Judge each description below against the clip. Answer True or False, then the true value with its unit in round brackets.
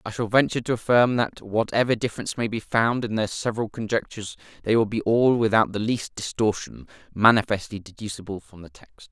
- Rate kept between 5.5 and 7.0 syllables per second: True (5.9 syllables/s)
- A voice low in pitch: True (110 Hz)